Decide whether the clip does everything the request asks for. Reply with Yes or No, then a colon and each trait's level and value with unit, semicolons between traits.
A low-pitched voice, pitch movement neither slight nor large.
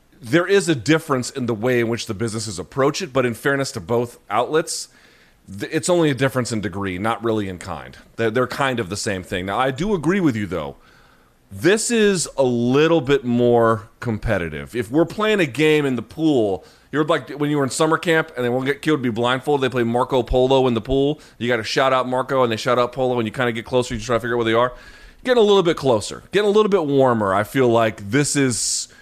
Yes: low, 125 Hz; average, 4.6 semitones